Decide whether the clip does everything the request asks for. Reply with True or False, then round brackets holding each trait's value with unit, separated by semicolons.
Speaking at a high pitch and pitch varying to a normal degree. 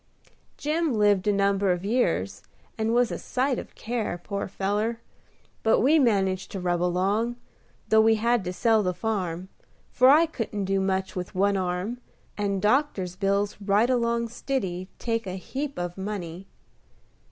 True (205 Hz; 3.8 semitones)